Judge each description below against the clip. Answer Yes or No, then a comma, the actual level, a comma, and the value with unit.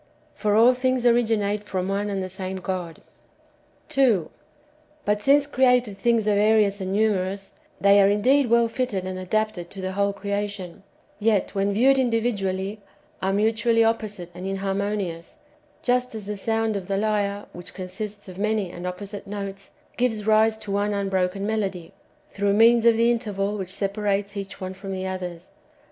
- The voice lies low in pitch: No, high, 205 Hz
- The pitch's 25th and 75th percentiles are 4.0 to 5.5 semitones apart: No, narrow, 2.4 semitones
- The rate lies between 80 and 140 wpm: No, average, 165 wpm